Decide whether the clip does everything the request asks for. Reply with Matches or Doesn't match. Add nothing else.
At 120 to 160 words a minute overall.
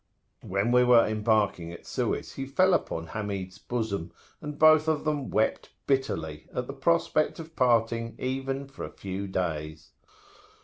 Matches